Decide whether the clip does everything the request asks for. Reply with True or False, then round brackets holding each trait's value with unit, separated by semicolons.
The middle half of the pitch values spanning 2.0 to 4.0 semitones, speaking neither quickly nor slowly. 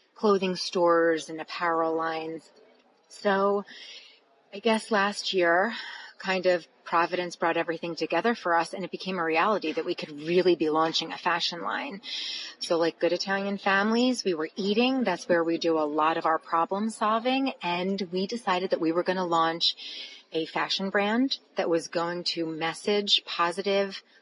True (3.3 semitones; 170 wpm)